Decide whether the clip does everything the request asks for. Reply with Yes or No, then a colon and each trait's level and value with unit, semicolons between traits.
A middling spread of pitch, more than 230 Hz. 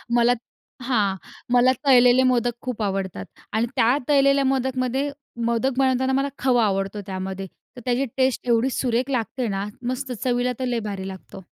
Yes: average, 3.4 semitones; high, 245 Hz